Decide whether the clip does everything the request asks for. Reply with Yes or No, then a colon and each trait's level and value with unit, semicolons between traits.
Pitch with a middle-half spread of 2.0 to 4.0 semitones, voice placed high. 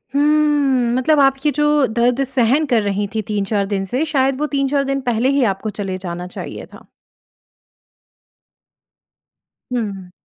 No: average, 5.2 semitones; very high, 250 Hz